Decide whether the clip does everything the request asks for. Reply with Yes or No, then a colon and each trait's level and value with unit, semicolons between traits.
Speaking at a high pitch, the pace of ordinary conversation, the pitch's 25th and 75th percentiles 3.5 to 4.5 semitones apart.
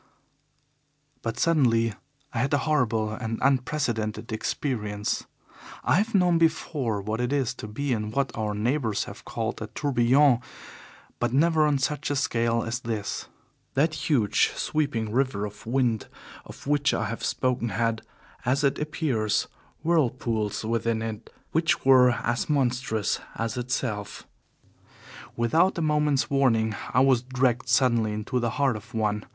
No: low, 125 Hz; average, 145 wpm; average, 4.0 semitones